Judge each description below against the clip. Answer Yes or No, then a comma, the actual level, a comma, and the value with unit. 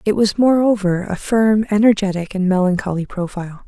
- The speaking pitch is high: Yes, high, 200 Hz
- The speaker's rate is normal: Yes, average, 145 wpm